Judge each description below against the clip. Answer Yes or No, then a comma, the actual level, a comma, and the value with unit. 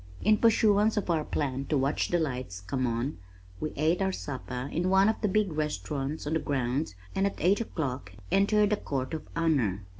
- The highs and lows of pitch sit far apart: Yes, wide, 6.7 semitones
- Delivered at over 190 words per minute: Yes, average, 200 wpm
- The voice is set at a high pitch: No, medium, 155 Hz